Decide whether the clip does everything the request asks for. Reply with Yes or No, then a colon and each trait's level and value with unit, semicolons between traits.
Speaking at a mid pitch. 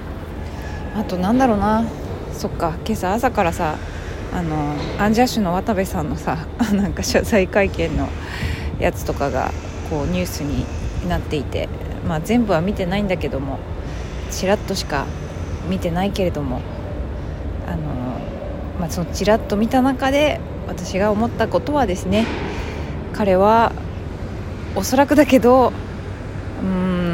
No: low, 100 Hz